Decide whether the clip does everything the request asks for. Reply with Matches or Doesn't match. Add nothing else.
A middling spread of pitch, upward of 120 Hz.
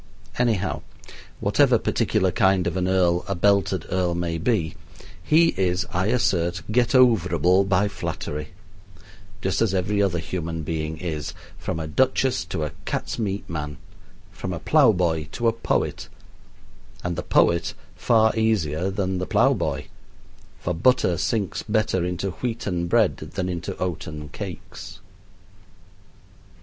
Doesn't match